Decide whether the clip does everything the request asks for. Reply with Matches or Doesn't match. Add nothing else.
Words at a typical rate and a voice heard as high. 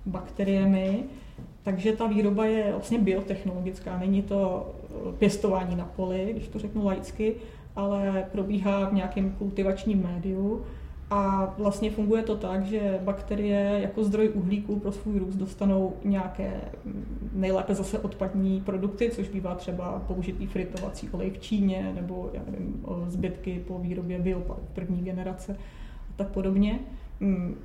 Doesn't match